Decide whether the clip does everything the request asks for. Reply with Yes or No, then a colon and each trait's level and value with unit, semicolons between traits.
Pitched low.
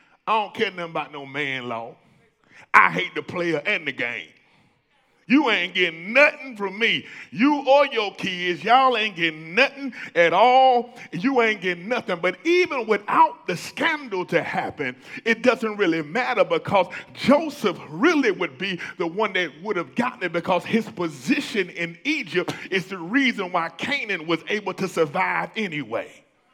No: high, 200 Hz